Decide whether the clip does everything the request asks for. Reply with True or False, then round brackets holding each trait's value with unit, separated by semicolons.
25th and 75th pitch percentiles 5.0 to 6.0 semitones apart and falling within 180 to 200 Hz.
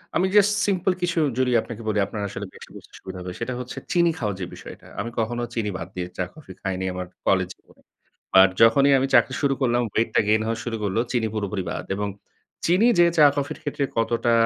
False (5.4 semitones; 115 Hz)